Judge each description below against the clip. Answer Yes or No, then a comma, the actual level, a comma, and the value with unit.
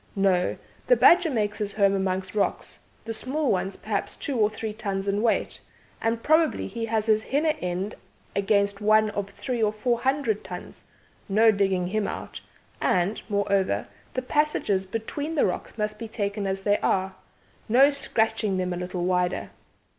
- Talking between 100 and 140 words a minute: No, average, 170 wpm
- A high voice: Yes, high, 210 Hz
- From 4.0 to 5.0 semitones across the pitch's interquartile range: No, average, 2.9 semitones